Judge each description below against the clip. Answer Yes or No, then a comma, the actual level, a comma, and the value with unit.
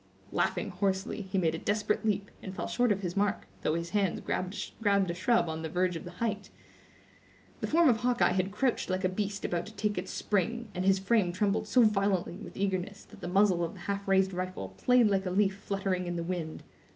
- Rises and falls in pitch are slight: Yes, narrow, 2.3 semitones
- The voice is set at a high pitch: Yes, high, 195 Hz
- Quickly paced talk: Yes, fast, 225 wpm